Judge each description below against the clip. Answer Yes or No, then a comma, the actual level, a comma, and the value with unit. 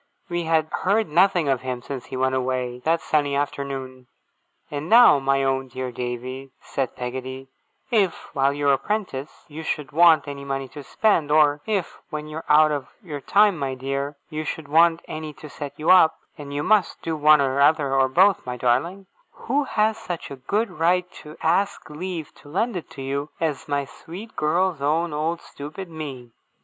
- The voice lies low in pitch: No, medium, 150 Hz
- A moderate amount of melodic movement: Yes, average, 3.9 semitones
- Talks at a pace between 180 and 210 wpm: Yes, average, 185 wpm